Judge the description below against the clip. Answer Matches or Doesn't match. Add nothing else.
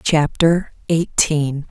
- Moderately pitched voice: Matches